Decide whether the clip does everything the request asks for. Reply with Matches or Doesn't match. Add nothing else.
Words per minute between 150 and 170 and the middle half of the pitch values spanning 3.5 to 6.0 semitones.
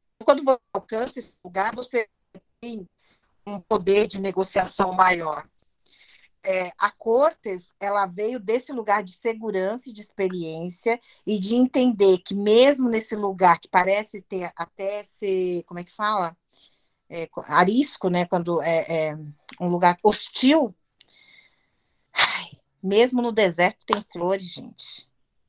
Doesn't match